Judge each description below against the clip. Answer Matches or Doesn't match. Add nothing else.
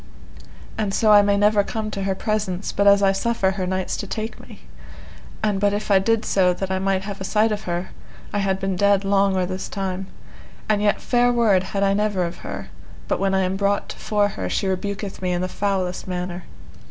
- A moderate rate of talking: Doesn't match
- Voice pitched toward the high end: Matches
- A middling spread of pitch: Doesn't match